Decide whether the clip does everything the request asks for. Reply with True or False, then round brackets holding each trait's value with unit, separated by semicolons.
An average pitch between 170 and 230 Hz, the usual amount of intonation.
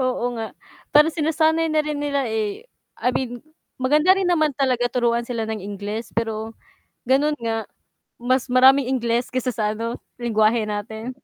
False (245 Hz; 4.3 semitones)